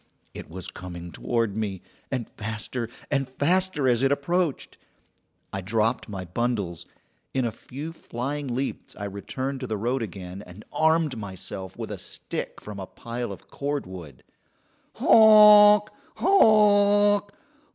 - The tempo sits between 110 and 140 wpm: Yes, slow, 135 wpm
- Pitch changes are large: Yes, wide, 7.6 semitones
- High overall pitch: No, low, 120 Hz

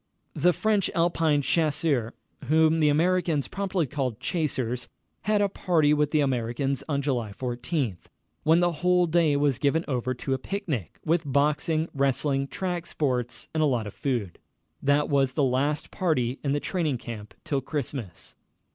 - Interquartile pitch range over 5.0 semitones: No, average, 4.0 semitones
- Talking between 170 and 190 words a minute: No, average, 160 wpm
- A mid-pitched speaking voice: Yes, medium, 145 Hz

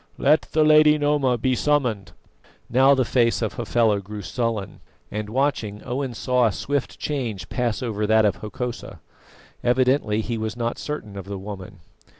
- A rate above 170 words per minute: No, average, 160 wpm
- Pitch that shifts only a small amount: No, average, 4.0 semitones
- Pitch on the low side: Yes, low, 120 Hz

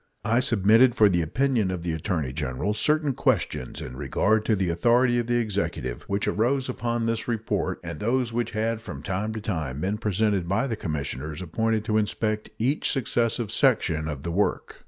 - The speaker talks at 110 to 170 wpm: No, average, 185 wpm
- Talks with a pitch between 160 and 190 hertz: No, low, 105 Hz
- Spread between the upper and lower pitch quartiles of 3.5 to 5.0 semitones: No, wide, 5.4 semitones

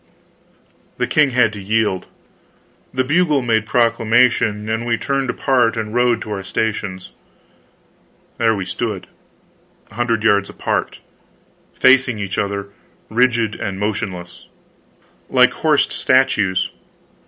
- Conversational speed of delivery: No, slow, 120 wpm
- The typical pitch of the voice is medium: No, low, 110 Hz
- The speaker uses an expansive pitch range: No, average, 3.3 semitones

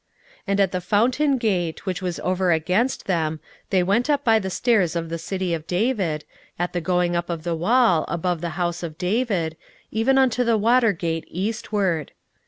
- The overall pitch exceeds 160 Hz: Yes, medium, 185 Hz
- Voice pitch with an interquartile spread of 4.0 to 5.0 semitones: Yes, average, 4.7 semitones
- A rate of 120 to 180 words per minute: No, average, 190 wpm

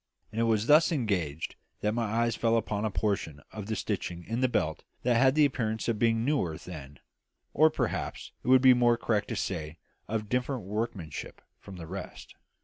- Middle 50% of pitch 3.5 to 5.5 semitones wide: Yes, average, 4.2 semitones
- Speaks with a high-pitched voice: No, low, 110 Hz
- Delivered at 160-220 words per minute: Yes, average, 200 wpm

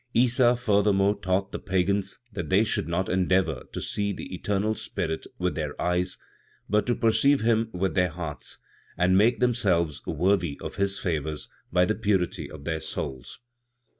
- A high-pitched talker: No, very low, 95 Hz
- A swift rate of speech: No, average, 165 wpm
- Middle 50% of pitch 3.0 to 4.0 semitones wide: Yes, average, 3.4 semitones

